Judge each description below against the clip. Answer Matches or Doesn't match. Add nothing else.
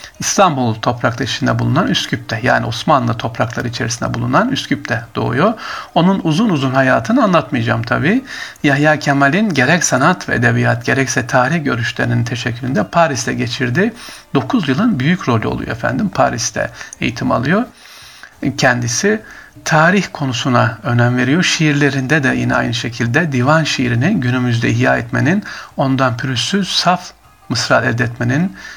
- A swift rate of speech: Doesn't match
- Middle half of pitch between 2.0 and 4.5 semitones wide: Doesn't match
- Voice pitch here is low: Matches